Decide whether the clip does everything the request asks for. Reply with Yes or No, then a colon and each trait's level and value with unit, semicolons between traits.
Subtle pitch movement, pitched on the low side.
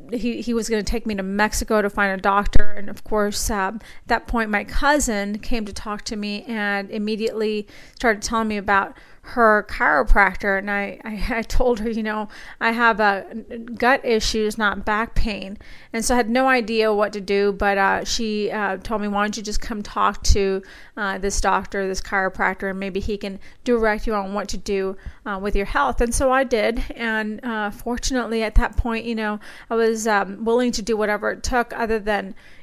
No: narrow, 2.1 semitones; high, 215 Hz